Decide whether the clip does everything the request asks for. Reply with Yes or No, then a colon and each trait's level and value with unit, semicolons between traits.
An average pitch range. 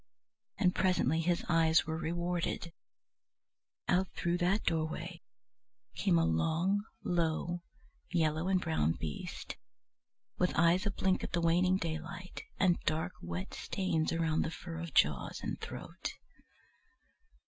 No: narrow, 2.2 semitones